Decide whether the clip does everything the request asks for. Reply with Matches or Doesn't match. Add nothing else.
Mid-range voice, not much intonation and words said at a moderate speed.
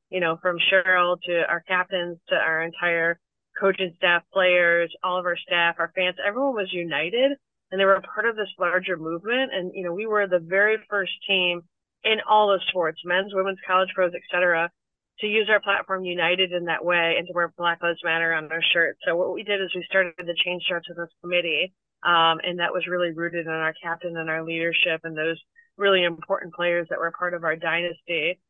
Doesn't match